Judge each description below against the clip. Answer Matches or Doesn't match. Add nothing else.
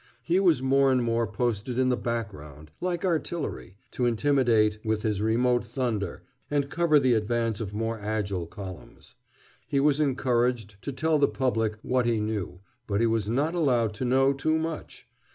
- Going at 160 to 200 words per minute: Matches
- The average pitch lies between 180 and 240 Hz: Doesn't match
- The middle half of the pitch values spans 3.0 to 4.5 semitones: Matches